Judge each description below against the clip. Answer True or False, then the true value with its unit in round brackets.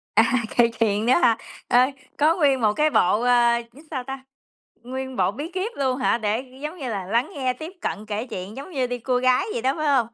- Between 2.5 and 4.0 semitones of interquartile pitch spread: True (3.2 semitones)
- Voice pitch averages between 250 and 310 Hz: True (255 Hz)